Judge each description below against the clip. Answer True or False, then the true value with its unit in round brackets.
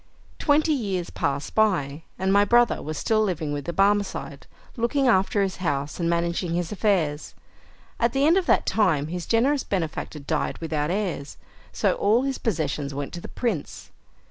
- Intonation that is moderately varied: False (6.1 semitones)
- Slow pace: False (170 wpm)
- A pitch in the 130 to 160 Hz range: False (185 Hz)